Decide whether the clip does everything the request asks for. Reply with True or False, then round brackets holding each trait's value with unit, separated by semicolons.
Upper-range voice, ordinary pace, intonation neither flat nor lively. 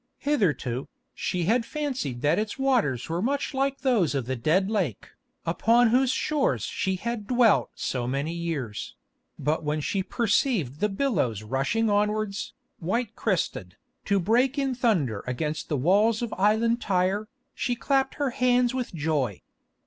False (205 Hz; 150 wpm; 8.3 semitones)